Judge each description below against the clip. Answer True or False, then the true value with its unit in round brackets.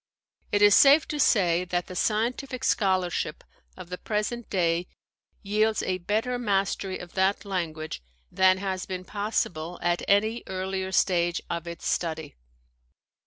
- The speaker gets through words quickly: False (140 wpm)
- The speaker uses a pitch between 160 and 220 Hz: True (190 Hz)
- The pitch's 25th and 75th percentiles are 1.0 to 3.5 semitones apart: True (3.1 semitones)